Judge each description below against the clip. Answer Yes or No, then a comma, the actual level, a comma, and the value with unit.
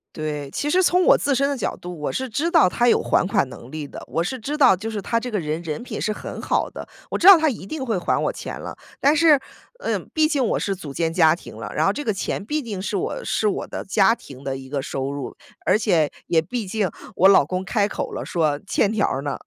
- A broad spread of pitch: Yes, wide, 8.3 semitones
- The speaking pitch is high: Yes, high, 200 Hz